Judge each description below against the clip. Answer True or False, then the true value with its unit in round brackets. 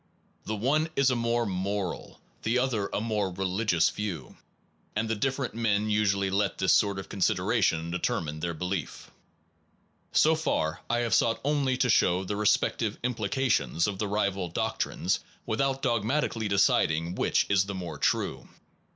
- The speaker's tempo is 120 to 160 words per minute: False (170 wpm)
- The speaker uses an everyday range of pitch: True (3.9 semitones)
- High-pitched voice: False (105 Hz)